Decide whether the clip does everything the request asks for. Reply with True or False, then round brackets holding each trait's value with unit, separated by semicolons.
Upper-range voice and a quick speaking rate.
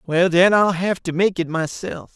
False (175 Hz; 220 wpm)